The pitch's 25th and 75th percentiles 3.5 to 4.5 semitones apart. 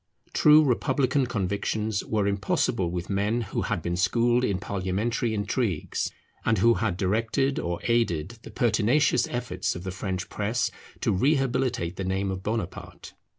Yes: average, 4.1 semitones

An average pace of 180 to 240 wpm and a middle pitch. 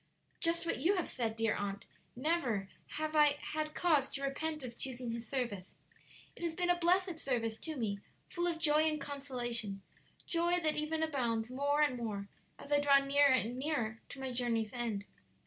No: average, 185 wpm; very high, 275 Hz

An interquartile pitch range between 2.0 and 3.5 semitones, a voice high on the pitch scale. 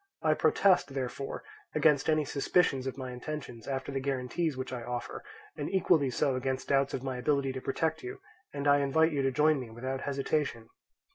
No: narrow, 2.5 semitones; low, 135 Hz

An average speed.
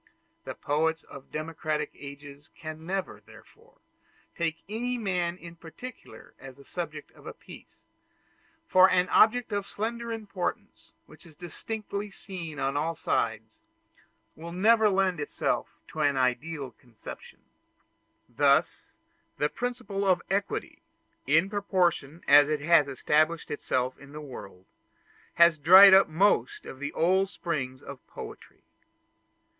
No: slow, 130 wpm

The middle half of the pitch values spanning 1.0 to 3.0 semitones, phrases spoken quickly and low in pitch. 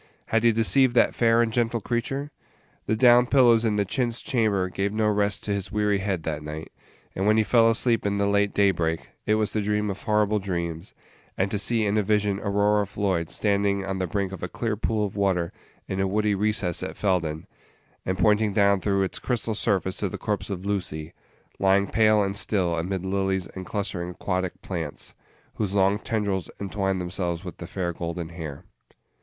No: narrow, 2.4 semitones; average, 195 wpm; low, 100 Hz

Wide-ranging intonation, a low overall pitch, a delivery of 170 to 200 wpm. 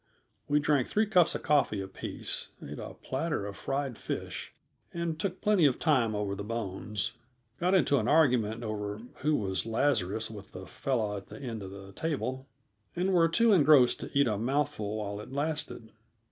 Yes: wide, 6.4 semitones; low, 125 Hz; average, 180 wpm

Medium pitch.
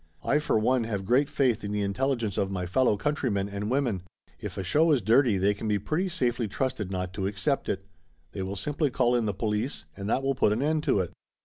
No: low, 110 Hz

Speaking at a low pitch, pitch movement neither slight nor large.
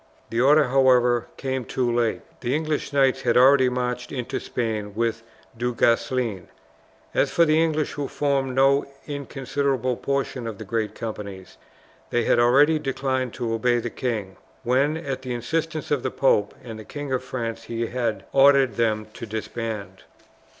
Yes: low, 125 Hz; average, 3.1 semitones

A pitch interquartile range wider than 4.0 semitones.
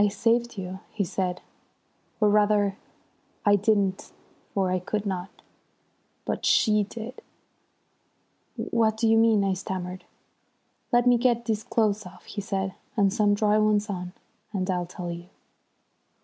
No: narrow, 2.6 semitones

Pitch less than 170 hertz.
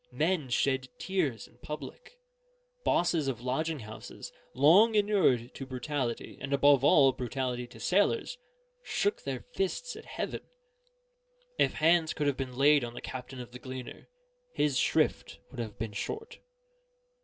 Yes: medium, 140 Hz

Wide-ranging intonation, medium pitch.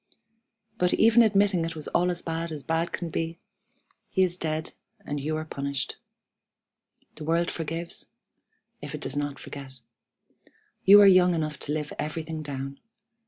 No: average, 2.7 semitones; medium, 165 Hz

